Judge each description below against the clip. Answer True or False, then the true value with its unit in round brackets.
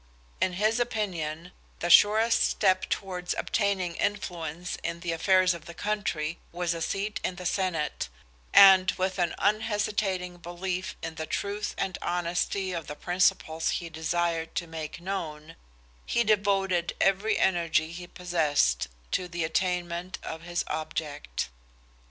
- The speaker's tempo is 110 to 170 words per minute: True (140 wpm)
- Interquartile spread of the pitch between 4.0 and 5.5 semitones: False (2.6 semitones)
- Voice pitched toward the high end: False (180 Hz)